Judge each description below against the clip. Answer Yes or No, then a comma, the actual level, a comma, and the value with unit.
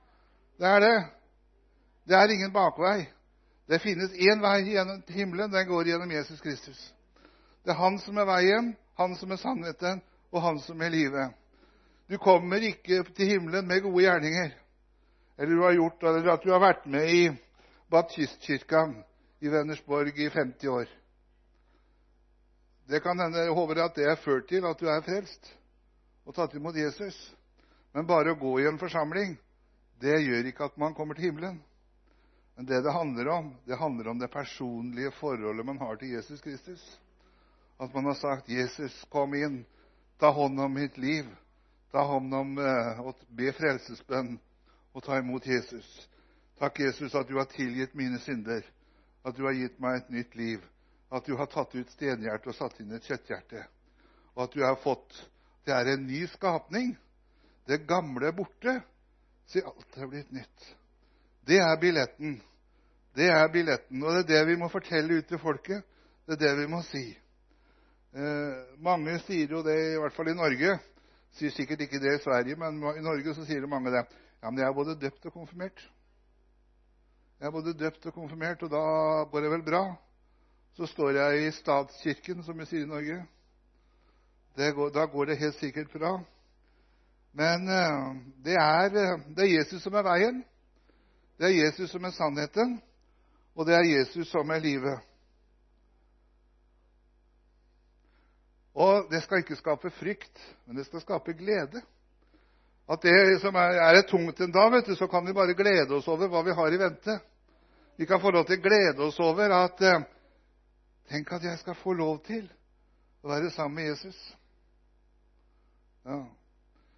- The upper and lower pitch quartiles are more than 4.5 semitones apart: Yes, average, 5.2 semitones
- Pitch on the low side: No, medium, 150 Hz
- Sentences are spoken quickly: No, average, 175 wpm